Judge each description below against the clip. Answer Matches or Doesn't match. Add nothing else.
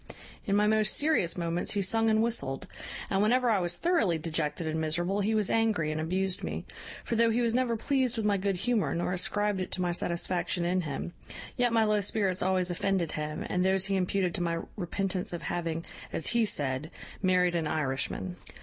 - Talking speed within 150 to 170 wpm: Doesn't match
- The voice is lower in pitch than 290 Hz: Matches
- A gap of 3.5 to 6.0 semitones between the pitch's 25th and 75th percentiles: Matches